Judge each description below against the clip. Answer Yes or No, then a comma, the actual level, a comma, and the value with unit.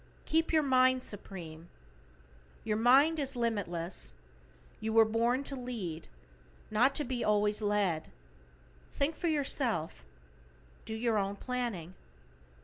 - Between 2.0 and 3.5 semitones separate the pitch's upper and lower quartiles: No, average, 4.4 semitones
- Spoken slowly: Yes, slow, 120 wpm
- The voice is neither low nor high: No, high, 225 Hz